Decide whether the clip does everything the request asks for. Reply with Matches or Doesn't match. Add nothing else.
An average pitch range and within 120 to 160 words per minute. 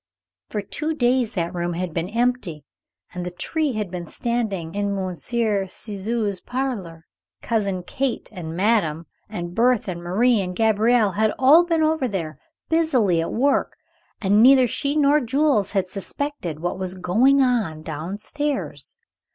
Doesn't match